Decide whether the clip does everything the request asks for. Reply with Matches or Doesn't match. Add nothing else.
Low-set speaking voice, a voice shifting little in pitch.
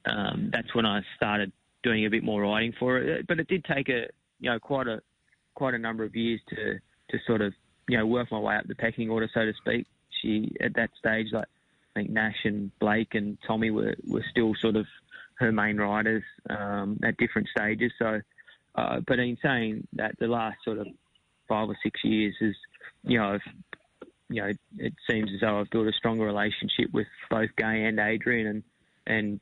Matches